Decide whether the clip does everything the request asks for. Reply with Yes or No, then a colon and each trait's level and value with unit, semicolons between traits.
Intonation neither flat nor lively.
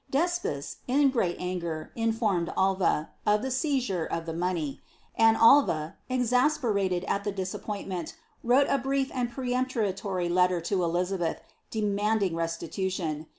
No: wide, 6.1 semitones